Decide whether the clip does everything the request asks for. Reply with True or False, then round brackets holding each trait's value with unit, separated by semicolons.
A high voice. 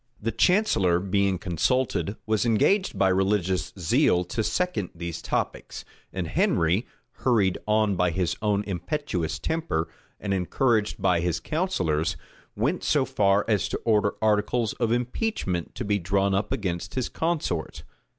False (100 Hz)